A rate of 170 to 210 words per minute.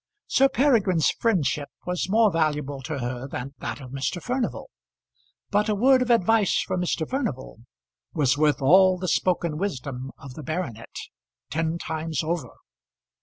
No: average, 150 wpm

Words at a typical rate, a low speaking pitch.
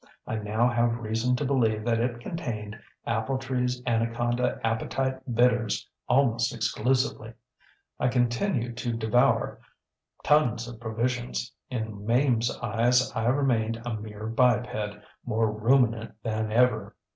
No: slow, 120 wpm; low, 120 Hz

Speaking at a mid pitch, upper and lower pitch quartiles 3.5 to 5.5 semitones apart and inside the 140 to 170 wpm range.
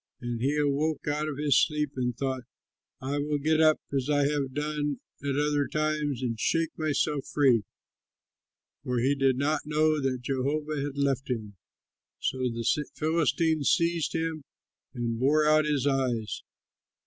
No: medium, 145 Hz; narrow, 2.5 semitones; average, 155 wpm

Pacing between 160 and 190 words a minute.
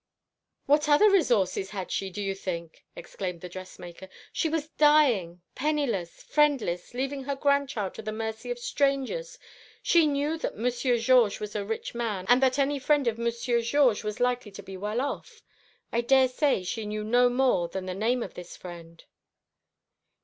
Yes: average, 170 wpm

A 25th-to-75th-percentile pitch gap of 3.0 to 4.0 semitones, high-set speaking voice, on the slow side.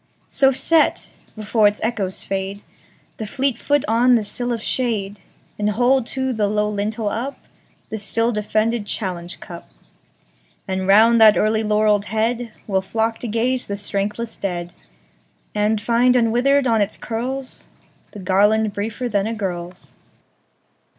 No: narrow, 2.6 semitones; high, 220 Hz; slow, 125 wpm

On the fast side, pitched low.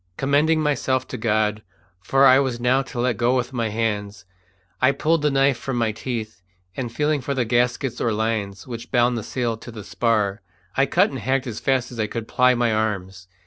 Yes: fast, 210 wpm; low, 120 Hz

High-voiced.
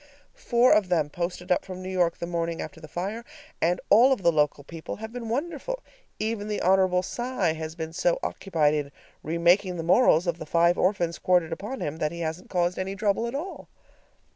No: medium, 180 Hz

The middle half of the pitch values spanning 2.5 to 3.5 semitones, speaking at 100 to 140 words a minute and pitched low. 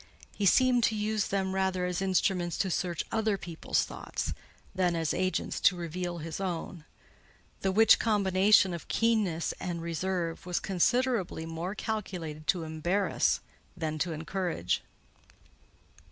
No: average, 2.8 semitones; slow, 135 wpm; medium, 185 Hz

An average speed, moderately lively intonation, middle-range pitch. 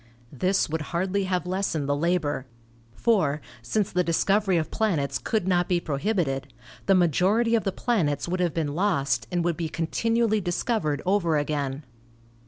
Yes: average, 160 wpm; average, 4.6 semitones; medium, 175 Hz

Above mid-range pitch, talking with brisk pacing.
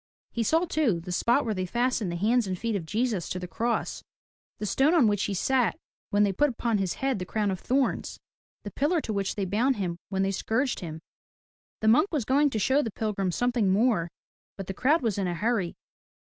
Yes: high, 215 Hz; fast, 225 wpm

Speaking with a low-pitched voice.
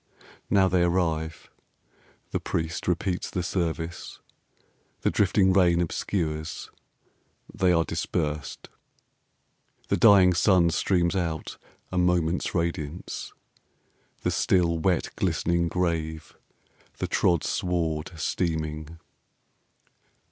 Yes: very low, 85 Hz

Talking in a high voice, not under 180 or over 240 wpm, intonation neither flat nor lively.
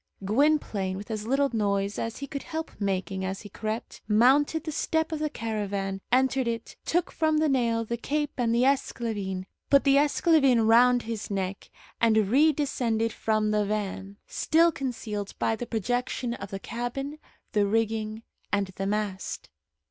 No: high, 230 Hz; average, 165 wpm; average, 4.8 semitones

